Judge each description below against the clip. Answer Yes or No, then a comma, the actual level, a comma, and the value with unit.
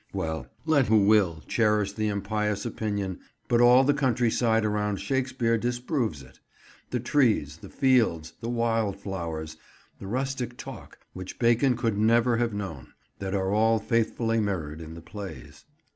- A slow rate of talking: No, average, 150 wpm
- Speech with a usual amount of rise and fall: Yes, average, 3.8 semitones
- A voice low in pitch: Yes, low, 110 Hz